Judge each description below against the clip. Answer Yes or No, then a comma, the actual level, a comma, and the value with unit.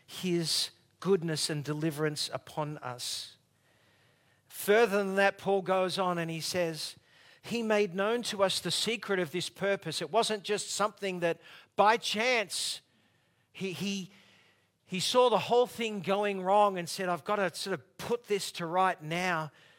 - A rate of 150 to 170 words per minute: Yes, average, 160 wpm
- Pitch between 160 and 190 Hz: Yes, medium, 185 Hz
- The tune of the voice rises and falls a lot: No, average, 4.4 semitones